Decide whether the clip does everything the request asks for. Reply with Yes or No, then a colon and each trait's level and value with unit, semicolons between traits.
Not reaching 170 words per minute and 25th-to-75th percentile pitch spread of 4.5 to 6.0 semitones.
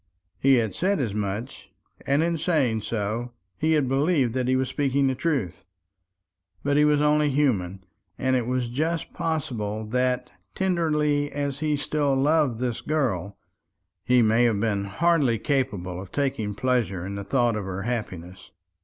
Yes: average, 160 wpm; average, 5.3 semitones